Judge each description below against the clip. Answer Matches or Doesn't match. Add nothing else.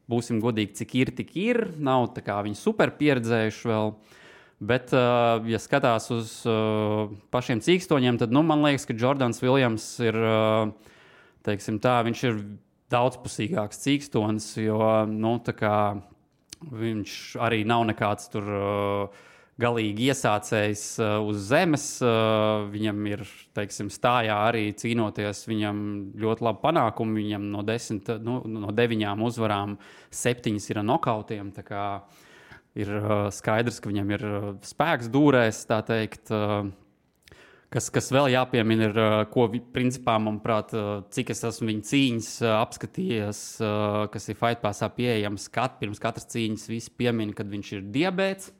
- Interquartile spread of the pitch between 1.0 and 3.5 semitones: Matches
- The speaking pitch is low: Matches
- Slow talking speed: Matches